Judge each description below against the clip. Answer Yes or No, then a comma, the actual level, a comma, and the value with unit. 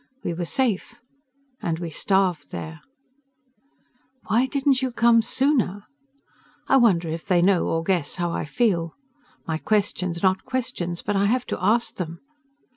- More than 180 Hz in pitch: Yes, high, 190 Hz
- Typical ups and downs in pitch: No, wide, 5.7 semitones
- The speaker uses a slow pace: No, average, 155 wpm